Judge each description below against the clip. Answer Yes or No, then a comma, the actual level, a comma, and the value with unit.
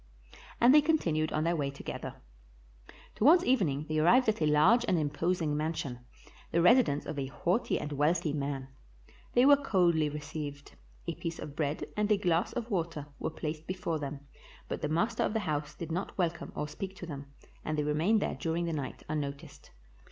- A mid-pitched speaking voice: Yes, medium, 160 Hz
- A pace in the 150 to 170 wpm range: No, average, 190 wpm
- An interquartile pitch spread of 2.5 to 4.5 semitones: Yes, average, 4.2 semitones